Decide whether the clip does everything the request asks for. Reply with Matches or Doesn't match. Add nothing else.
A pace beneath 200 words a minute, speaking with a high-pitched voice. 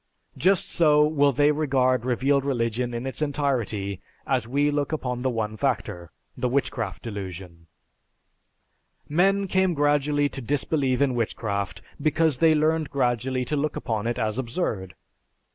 Doesn't match